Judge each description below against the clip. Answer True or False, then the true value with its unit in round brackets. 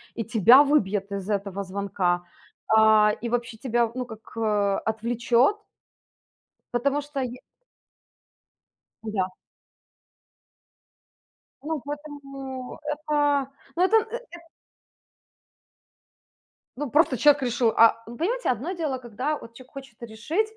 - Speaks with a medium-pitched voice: False (245 Hz)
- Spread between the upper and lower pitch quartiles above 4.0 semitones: True (4.9 semitones)